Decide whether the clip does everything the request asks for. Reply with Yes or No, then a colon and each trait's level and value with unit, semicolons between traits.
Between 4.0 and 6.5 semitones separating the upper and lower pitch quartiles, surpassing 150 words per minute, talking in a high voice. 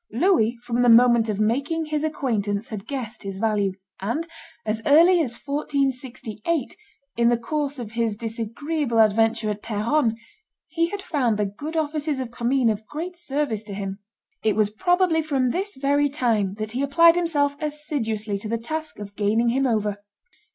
Yes: wide, 5.5 semitones; average, 170 wpm; high, 240 Hz